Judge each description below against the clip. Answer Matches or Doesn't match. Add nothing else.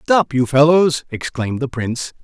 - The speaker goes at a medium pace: Matches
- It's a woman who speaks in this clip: Doesn't match